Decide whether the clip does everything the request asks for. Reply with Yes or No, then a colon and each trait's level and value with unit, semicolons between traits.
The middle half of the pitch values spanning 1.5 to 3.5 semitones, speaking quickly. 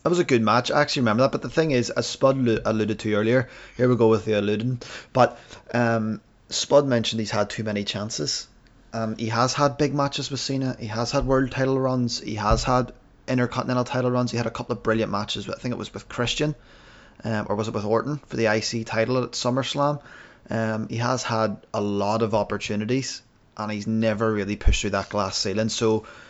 Yes: average, 2.8 semitones; fast, 220 wpm